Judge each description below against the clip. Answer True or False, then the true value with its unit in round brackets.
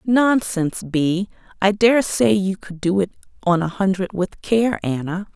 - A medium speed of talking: True (170 wpm)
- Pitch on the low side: False (195 Hz)